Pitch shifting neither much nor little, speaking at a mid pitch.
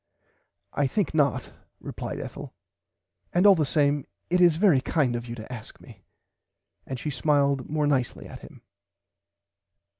Yes: average, 3.5 semitones; medium, 145 Hz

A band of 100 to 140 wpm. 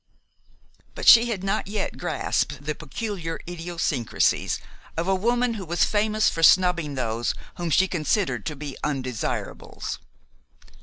Yes: slow, 135 wpm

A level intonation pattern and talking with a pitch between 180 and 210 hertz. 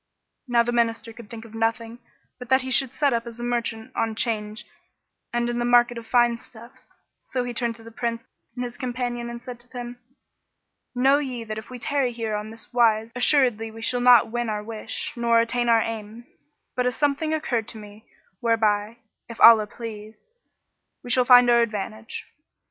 No: narrow, 1.5 semitones; high, 235 Hz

